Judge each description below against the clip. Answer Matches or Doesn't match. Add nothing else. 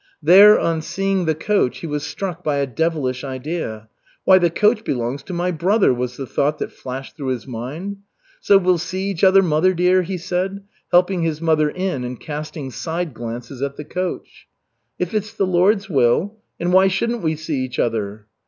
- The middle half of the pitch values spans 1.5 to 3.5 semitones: Doesn't match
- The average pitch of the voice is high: Doesn't match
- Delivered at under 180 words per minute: Doesn't match